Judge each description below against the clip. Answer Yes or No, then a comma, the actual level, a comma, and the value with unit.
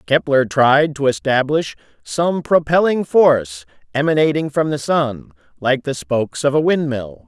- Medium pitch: Yes, medium, 145 Hz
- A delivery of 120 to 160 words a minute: Yes, average, 140 wpm